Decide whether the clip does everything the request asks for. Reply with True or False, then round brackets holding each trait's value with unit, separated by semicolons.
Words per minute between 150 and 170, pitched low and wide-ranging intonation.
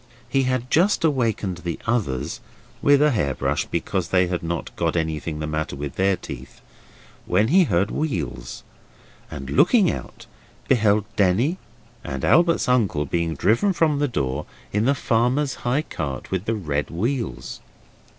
True (155 wpm; 100 Hz; 8.9 semitones)